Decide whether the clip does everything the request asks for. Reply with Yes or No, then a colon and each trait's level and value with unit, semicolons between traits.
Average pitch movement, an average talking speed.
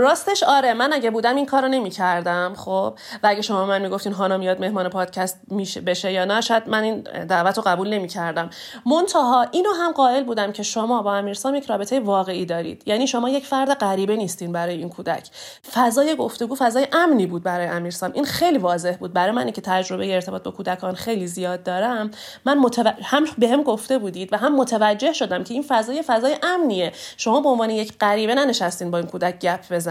No: wide, 6.2 semitones; average, 195 wpm